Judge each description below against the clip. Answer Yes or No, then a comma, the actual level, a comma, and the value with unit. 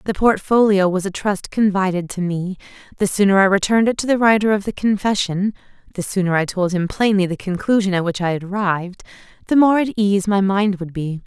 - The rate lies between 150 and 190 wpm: No, average, 200 wpm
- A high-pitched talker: Yes, high, 195 Hz